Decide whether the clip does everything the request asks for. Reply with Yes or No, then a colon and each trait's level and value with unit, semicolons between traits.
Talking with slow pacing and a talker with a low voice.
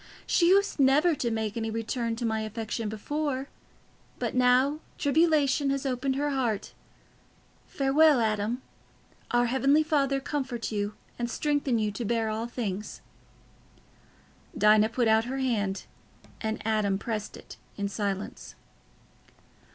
No: slow, 130 wpm; high, 240 Hz